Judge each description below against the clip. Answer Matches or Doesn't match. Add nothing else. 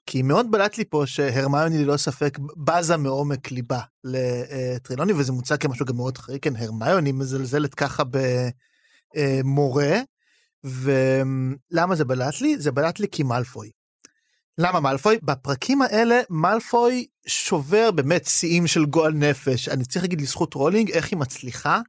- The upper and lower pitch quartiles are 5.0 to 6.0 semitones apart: Doesn't match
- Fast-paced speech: Doesn't match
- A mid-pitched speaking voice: Matches